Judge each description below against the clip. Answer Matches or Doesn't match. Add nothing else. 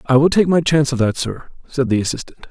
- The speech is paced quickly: Matches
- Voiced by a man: Matches